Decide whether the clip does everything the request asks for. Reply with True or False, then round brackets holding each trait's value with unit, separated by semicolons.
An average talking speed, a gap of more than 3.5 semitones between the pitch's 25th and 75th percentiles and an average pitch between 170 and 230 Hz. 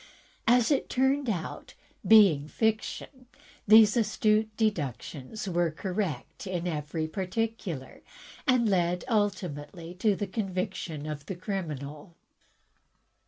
False (105 wpm; 5.1 semitones; 190 Hz)